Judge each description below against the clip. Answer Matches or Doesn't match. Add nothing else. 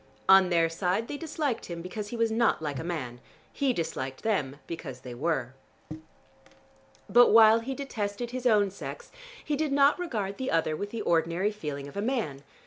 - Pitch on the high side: Matches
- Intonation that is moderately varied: Doesn't match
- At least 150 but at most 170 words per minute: Doesn't match